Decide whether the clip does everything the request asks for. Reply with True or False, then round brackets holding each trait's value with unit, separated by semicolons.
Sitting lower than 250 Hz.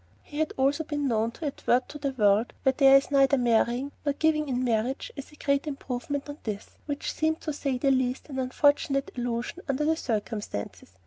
False (275 Hz)